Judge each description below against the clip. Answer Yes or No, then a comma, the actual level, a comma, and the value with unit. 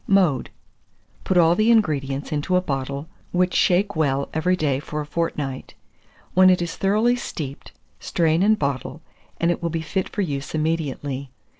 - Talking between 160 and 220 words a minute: Yes, average, 165 wpm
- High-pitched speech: No, medium, 160 Hz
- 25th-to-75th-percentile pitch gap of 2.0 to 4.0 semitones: No, average, 4.6 semitones